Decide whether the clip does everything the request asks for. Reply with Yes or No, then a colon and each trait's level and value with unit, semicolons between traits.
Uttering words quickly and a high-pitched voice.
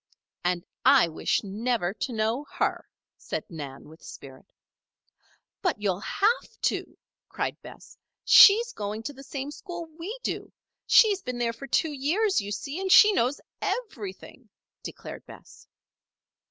No: average, 140 wpm; very high, 255 Hz